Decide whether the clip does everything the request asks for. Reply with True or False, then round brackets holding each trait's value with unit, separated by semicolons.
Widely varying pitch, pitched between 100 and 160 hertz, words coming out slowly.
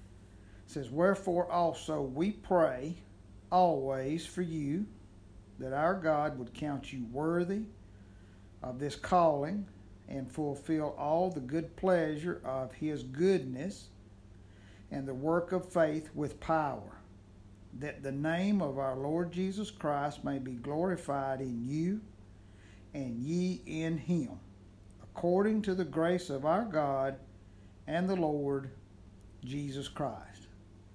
True (8.4 semitones; 140 Hz; 125 wpm)